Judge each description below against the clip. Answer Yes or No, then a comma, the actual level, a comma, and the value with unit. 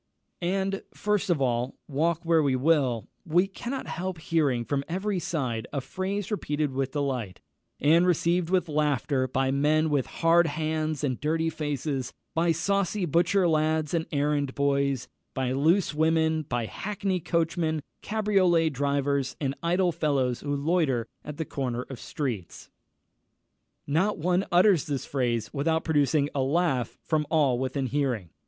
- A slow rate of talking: No, average, 145 wpm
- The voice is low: No, medium, 155 Hz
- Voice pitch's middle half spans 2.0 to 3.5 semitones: No, average, 3.9 semitones